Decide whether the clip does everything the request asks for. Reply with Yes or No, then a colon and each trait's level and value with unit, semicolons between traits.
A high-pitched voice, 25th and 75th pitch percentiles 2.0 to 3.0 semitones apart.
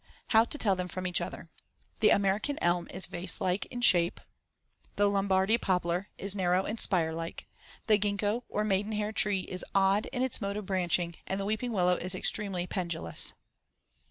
Yes: high, 195 Hz; narrow, 2.5 semitones